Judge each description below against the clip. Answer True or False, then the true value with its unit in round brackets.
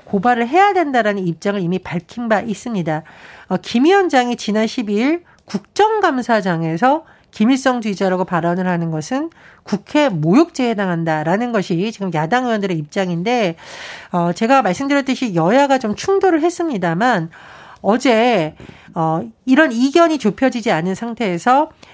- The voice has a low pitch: False (220 Hz)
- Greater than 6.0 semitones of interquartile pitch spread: True (6.4 semitones)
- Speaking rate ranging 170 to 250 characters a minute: False (320 characters per minute)